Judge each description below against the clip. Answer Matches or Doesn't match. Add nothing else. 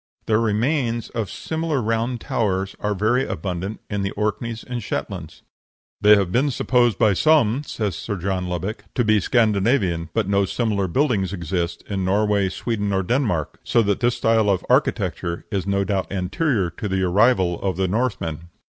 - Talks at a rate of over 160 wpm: Matches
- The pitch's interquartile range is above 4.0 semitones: Doesn't match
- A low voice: Matches